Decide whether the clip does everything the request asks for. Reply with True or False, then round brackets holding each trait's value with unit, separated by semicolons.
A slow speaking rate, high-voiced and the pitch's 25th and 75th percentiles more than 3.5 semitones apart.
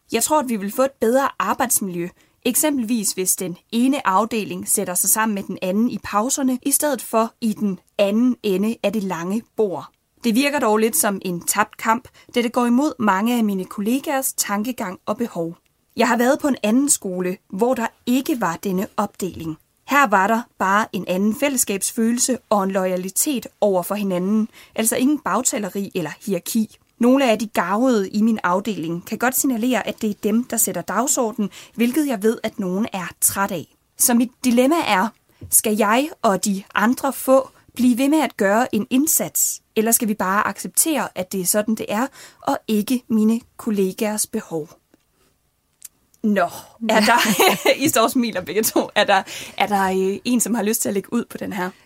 False (190 wpm; 220 Hz; 4.0 semitones)